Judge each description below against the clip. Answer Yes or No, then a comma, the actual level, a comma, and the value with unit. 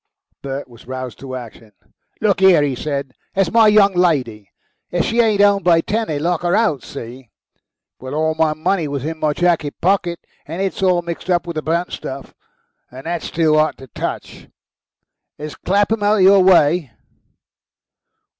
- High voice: No, medium, 165 Hz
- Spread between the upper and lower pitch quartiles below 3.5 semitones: No, average, 5.2 semitones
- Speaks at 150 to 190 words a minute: Yes, average, 175 wpm